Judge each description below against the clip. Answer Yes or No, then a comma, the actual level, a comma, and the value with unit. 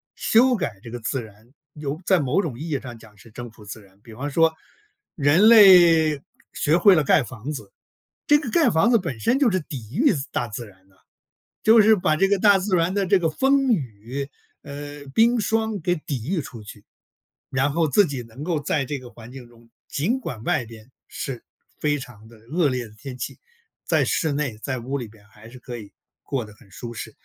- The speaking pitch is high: No, medium, 140 Hz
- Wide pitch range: Yes, wide, 7.4 semitones